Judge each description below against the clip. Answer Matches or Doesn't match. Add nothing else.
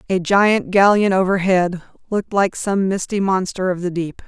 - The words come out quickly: Doesn't match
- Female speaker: Matches